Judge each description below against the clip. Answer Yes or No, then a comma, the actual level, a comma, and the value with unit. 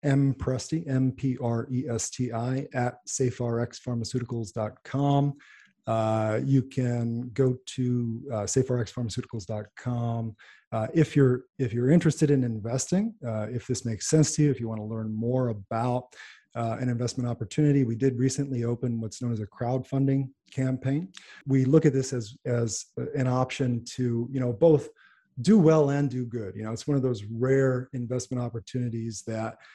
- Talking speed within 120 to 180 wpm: Yes, average, 160 wpm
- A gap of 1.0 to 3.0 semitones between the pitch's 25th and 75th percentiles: Yes, narrow, 2.6 semitones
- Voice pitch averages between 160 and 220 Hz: No, low, 125 Hz